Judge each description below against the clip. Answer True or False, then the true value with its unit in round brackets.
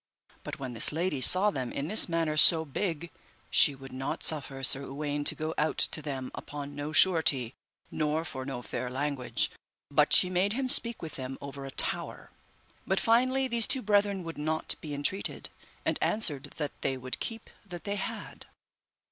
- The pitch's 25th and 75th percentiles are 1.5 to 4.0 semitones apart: False (5.4 semitones)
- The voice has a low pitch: False (155 Hz)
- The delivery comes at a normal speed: True (180 wpm)